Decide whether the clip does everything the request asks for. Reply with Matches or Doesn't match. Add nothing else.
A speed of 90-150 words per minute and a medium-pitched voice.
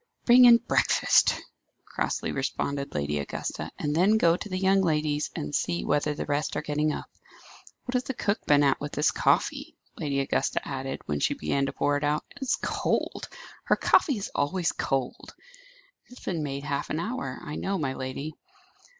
Doesn't match